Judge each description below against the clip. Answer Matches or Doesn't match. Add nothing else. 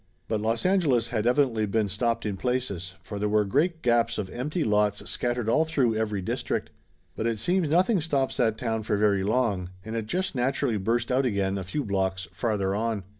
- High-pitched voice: Doesn't match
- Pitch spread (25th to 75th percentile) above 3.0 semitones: Matches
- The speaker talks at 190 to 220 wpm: Matches